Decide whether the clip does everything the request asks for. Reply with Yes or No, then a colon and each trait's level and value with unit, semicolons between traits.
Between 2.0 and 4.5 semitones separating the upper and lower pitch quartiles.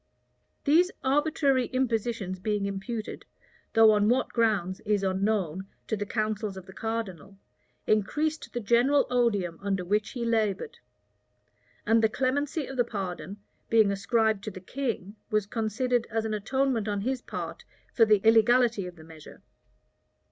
Yes: average, 3.5 semitones